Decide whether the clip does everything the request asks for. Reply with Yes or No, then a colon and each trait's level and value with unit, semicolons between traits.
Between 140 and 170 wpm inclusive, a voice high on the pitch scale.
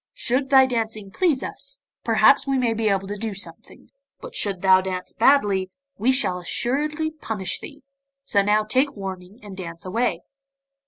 Yes: average, 165 wpm; high, 220 Hz